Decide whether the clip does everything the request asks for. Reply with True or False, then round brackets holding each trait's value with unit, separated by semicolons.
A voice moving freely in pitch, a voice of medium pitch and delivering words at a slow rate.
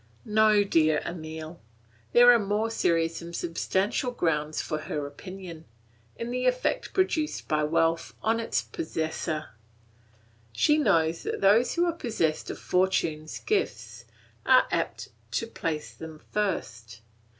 True (6.3 semitones; 170 Hz; 130 wpm)